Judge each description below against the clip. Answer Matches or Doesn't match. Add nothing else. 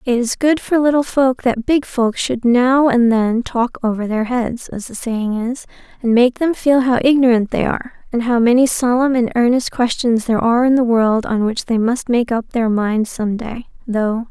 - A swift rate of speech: Matches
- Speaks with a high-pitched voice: Matches